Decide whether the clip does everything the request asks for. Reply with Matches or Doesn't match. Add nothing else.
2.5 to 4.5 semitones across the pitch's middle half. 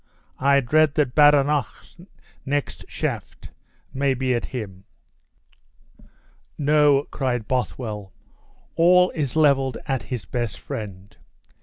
Matches